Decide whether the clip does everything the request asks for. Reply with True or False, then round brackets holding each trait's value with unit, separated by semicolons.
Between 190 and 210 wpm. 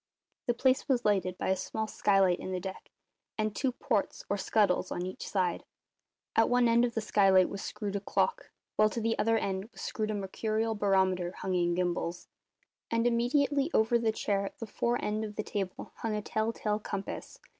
True (200 wpm)